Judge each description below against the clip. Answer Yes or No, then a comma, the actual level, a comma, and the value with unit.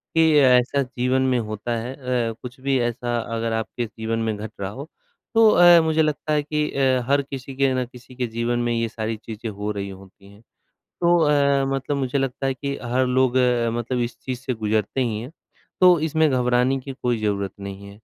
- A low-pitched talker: Yes, low, 125 Hz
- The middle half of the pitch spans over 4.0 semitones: No, average, 3.4 semitones